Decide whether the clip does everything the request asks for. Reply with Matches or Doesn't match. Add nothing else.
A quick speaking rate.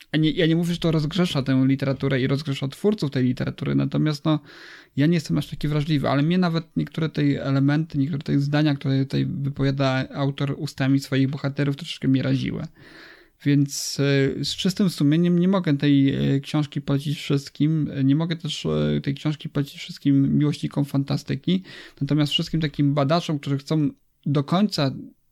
Matches